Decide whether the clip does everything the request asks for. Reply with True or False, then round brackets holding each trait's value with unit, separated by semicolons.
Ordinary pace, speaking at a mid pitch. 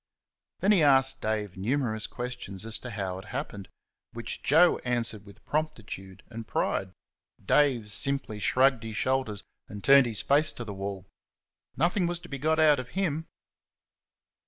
False (160 wpm; 120 Hz)